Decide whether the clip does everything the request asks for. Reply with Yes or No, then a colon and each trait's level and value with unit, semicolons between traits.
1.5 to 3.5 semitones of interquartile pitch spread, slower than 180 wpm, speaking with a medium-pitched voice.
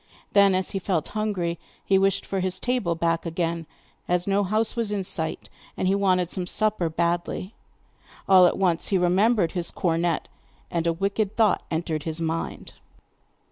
Yes: average, 2.8 semitones; average, 170 wpm; medium, 180 Hz